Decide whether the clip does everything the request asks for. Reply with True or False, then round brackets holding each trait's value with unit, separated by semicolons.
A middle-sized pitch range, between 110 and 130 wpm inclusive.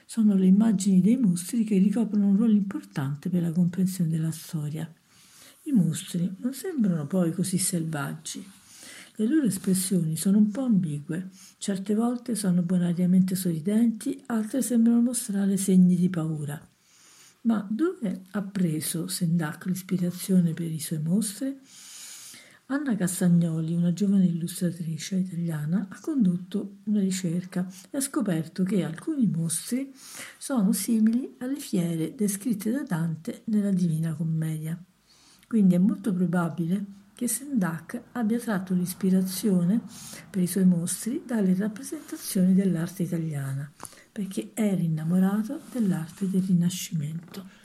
True (3.8 semitones; 125 wpm)